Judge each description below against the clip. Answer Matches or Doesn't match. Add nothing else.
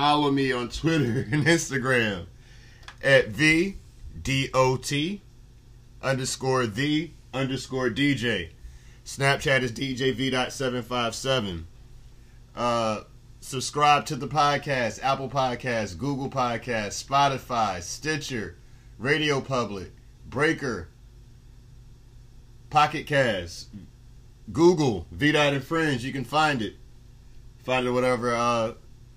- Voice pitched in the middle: Doesn't match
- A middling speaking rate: Doesn't match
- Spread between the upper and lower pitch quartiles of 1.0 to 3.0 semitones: Matches